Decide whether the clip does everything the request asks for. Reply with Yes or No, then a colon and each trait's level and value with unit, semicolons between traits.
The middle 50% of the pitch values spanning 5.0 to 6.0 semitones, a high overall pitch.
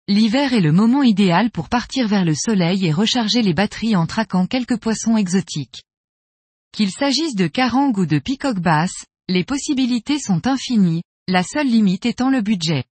Yes: average, 5.3 semitones; high, 215 Hz